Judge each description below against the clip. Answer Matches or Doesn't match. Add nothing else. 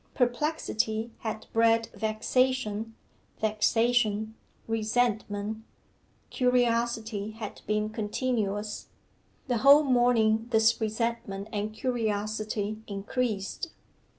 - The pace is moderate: Doesn't match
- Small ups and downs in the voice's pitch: Matches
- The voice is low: Doesn't match